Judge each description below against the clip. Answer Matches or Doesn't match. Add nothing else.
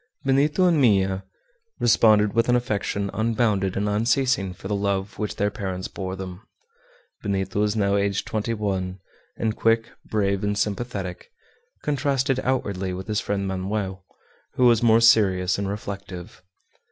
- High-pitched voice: Doesn't match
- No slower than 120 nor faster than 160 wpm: Matches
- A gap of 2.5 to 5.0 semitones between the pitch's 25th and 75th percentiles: Matches